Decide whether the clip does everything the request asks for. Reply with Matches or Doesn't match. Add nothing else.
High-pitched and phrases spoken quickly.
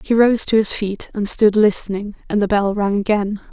Matches